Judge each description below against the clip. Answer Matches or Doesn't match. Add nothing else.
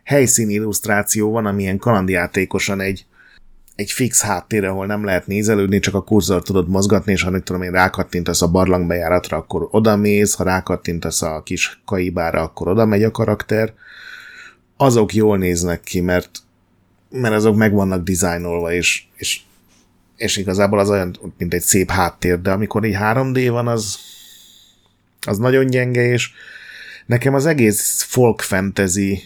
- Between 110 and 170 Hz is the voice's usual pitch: Doesn't match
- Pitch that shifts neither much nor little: Matches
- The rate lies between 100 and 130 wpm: Doesn't match